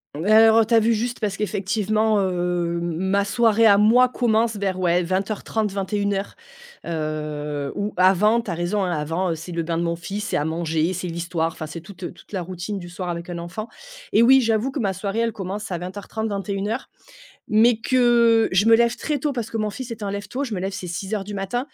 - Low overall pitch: No, high, 200 Hz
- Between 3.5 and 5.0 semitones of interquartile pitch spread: Yes, average, 4.0 semitones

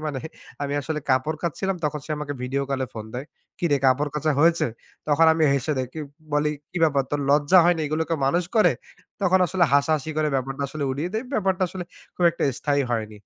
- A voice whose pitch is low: No, medium, 150 Hz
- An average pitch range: Yes, average, 3.3 semitones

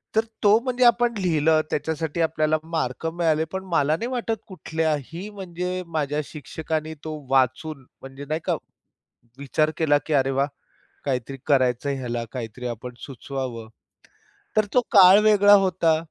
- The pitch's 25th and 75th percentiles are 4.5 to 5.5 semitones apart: Yes, average, 4.9 semitones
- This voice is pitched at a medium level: Yes, medium, 155 Hz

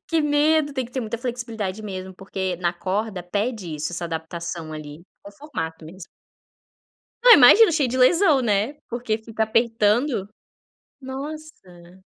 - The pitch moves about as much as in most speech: No, wide, 6.4 semitones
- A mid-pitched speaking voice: No, high, 220 Hz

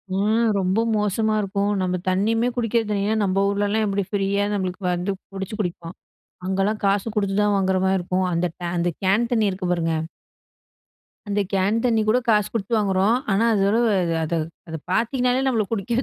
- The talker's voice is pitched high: Yes, high, 200 Hz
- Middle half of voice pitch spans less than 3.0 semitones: Yes, narrow, 2.5 semitones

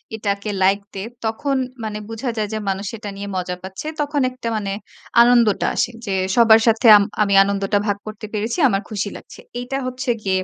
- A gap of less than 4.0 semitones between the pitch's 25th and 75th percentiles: Yes, average, 2.8 semitones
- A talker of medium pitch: No, high, 215 Hz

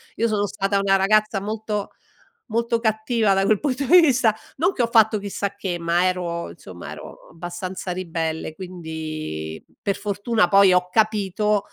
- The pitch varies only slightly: No, average, 3.5 semitones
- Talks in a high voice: Yes, high, 200 Hz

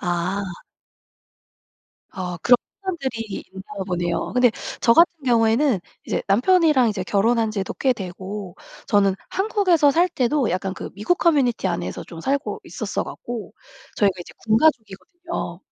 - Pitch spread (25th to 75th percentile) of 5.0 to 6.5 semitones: No, wide, 6.9 semitones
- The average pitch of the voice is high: Yes, high, 225 Hz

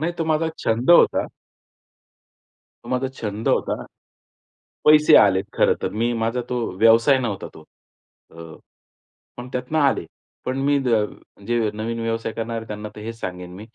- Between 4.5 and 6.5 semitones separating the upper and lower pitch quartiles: No, average, 3.6 semitones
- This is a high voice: No, low, 115 Hz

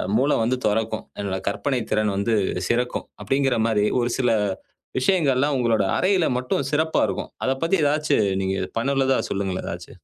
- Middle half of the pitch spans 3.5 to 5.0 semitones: Yes, average, 4.2 semitones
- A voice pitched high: No, low, 125 Hz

